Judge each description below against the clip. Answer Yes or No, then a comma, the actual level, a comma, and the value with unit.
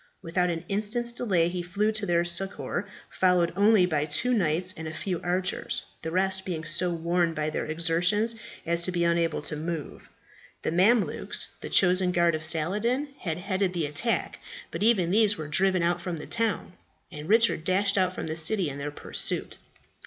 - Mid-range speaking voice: Yes, medium, 180 Hz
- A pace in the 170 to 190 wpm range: Yes, average, 185 wpm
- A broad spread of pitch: No, average, 3.2 semitones